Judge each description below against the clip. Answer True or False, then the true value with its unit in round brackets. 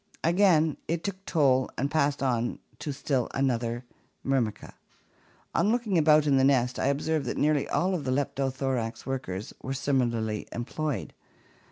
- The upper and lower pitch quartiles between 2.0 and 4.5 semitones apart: True (3.5 semitones)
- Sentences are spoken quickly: False (145 wpm)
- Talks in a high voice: False (135 Hz)